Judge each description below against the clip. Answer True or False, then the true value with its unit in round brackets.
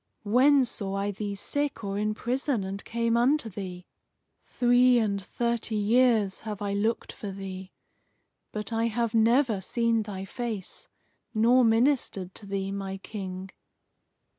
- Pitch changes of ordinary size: True (3.2 semitones)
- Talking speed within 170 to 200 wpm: False (140 wpm)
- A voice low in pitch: False (215 Hz)